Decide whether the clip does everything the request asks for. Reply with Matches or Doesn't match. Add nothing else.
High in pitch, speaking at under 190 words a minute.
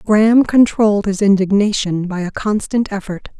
Matches